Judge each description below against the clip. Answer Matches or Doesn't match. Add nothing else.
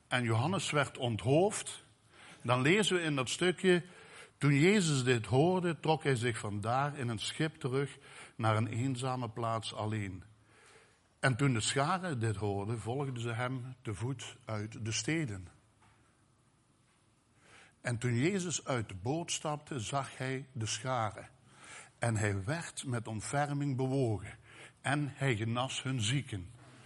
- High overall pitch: Doesn't match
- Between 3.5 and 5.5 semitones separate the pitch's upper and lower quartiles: Matches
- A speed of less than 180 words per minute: Matches